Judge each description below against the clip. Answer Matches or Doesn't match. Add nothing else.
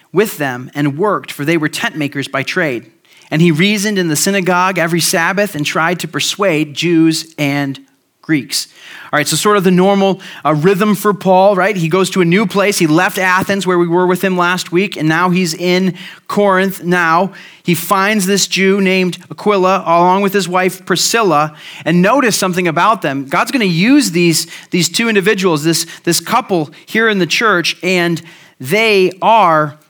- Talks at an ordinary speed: Matches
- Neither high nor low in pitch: Matches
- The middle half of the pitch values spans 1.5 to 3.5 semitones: Matches